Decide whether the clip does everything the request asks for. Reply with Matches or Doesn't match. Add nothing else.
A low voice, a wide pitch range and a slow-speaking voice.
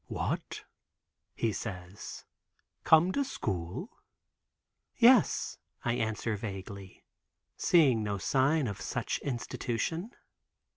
Matches